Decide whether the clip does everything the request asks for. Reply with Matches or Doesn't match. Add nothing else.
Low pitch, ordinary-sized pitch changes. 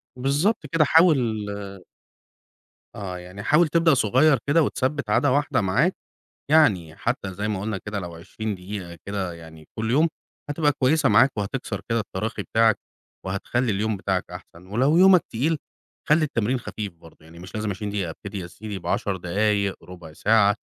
Doesn't match